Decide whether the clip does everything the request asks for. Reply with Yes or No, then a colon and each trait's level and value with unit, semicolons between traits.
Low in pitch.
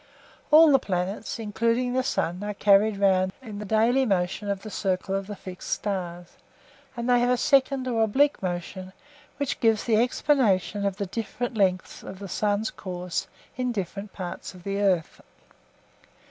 No: high, 205 Hz